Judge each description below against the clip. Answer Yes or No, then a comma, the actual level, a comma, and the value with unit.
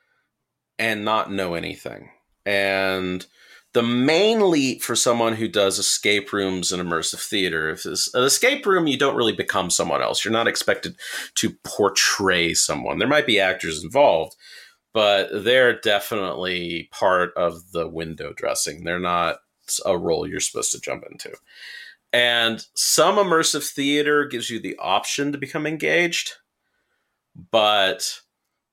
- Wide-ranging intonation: Yes, wide, 6.3 semitones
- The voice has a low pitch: Yes, low, 105 Hz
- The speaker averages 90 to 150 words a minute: Yes, average, 140 wpm